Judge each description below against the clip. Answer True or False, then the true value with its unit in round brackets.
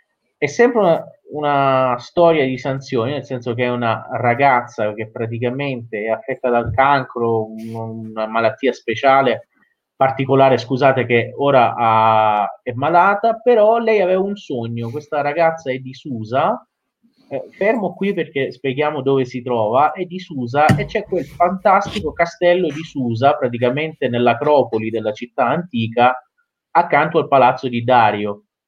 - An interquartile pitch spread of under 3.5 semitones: False (5.0 semitones)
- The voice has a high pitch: False (130 Hz)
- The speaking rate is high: False (140 wpm)